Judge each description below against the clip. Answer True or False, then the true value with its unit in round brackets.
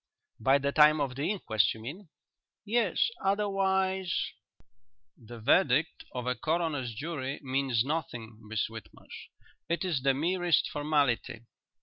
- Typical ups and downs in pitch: False (6.0 semitones)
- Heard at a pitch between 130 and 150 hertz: True (140 Hz)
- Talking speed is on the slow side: True (130 wpm)